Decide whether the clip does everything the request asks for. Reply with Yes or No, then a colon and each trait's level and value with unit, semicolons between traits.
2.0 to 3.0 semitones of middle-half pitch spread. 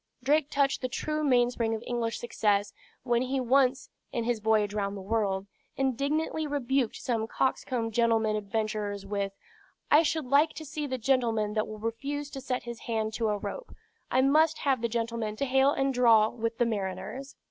No: average, 3.9 semitones